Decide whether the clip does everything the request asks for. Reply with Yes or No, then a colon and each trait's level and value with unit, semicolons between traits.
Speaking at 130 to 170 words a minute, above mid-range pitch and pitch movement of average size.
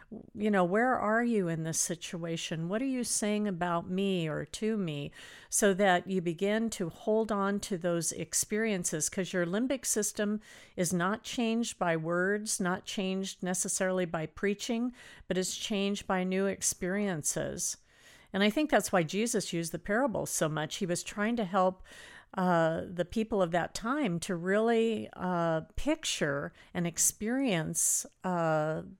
Yes: average, 155 wpm; high, 195 Hz; average, 3.4 semitones